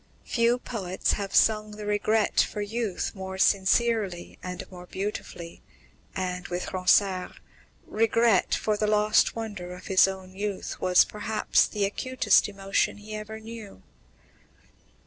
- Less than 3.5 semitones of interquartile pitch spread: Yes, narrow, 2.5 semitones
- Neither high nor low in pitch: No, high, 205 Hz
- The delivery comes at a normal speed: No, slow, 130 wpm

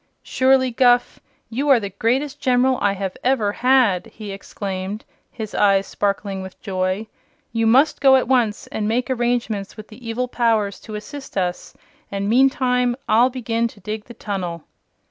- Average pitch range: Yes, average, 3.9 semitones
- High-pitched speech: Yes, high, 225 Hz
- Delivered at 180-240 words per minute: No, average, 165 wpm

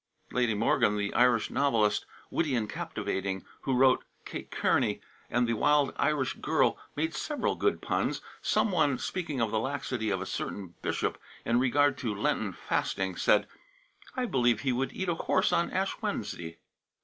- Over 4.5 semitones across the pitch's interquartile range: Yes, average, 5.2 semitones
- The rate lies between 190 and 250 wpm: No, average, 165 wpm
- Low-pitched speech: Yes, low, 125 Hz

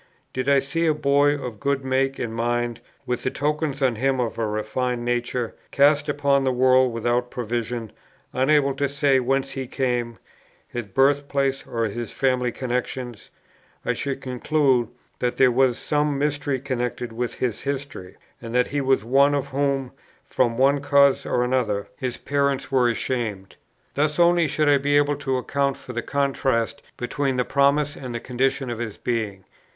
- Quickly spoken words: No, average, 175 wpm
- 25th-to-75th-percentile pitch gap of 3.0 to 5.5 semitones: No, narrow, 2.6 semitones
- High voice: No, low, 130 Hz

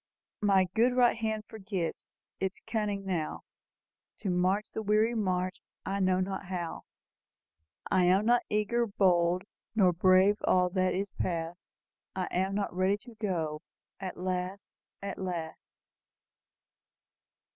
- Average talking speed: No, slow, 130 wpm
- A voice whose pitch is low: No, high, 190 Hz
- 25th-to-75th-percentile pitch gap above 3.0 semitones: No, narrow, 2.5 semitones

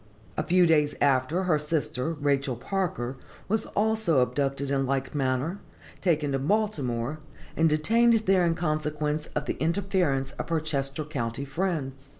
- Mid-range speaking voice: Yes, medium, 150 Hz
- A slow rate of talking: No, average, 150 wpm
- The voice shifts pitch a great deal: No, average, 4.2 semitones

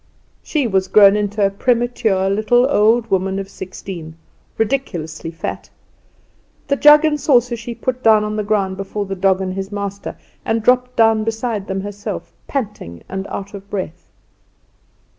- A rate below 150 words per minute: No, average, 160 wpm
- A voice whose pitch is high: Yes, high, 205 Hz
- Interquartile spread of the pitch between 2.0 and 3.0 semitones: No, average, 3.4 semitones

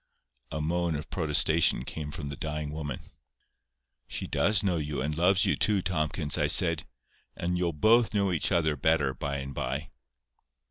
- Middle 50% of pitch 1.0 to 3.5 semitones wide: Yes, average, 3.2 semitones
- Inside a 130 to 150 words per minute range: No, average, 170 wpm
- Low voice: Yes, very low, 80 Hz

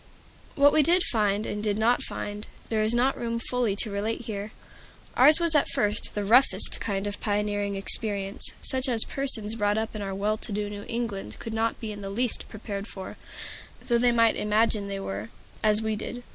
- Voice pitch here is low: No, high, 215 Hz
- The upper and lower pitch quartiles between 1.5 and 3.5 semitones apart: Yes, narrow, 2.4 semitones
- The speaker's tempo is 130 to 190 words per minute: No, average, 200 wpm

